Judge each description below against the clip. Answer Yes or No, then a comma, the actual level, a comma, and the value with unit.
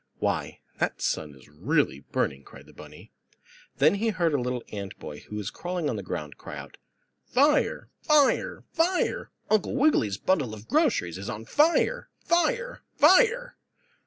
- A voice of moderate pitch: Yes, medium, 165 Hz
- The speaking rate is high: No, average, 160 wpm